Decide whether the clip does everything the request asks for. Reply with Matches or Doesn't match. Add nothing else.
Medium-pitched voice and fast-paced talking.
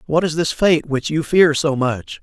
Matches